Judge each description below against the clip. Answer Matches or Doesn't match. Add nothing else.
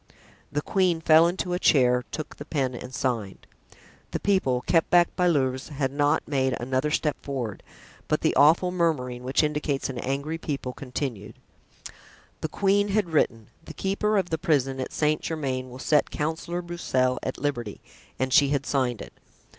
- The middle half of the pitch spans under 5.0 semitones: Matches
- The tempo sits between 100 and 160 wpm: Doesn't match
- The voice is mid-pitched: Matches